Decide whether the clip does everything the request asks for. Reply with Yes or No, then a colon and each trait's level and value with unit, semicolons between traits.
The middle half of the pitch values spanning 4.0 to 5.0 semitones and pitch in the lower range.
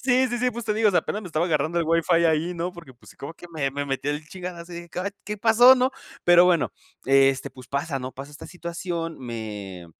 No: average, 4.6 semitones; medium, 170 Hz